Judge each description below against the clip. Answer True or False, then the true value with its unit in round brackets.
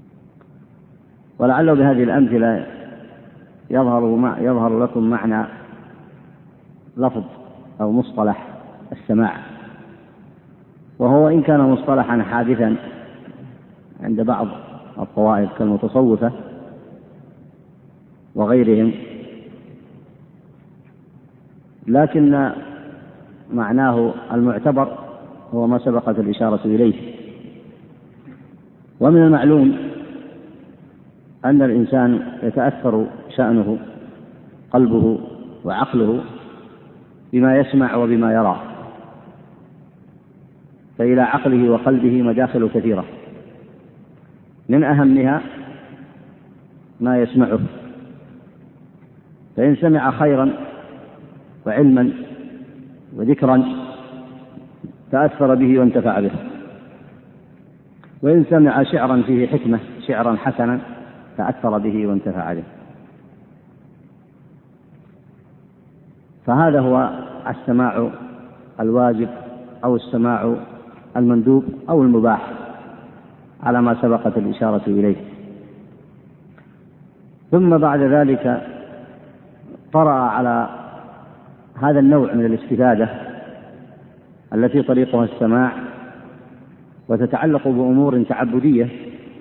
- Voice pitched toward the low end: True (125 Hz)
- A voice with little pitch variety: False (3.1 semitones)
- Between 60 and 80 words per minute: True (65 wpm)